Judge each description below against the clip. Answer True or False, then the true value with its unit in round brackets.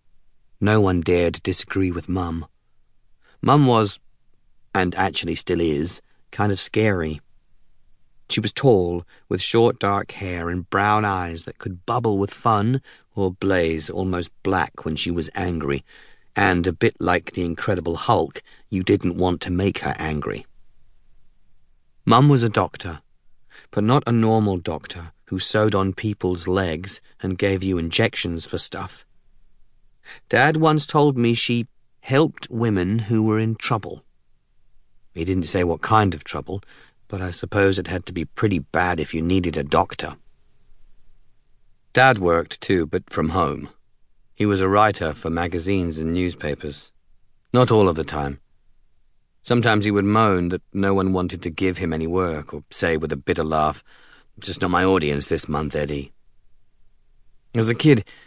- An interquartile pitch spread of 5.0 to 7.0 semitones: False (4.2 semitones)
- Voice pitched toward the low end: True (95 Hz)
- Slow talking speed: False (155 wpm)